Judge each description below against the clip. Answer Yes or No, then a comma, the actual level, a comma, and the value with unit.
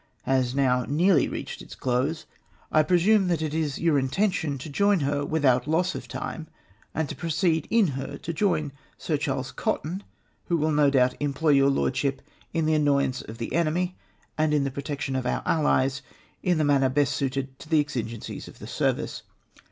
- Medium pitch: Yes, medium, 145 Hz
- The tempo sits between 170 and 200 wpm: Yes, average, 185 wpm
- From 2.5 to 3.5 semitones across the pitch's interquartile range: Yes, average, 3.2 semitones